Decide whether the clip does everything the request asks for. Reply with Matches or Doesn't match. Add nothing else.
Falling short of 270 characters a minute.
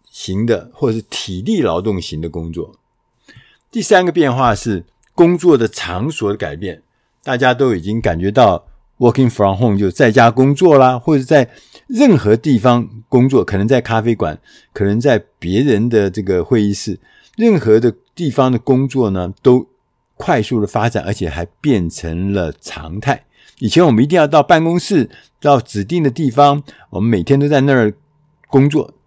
Doesn't match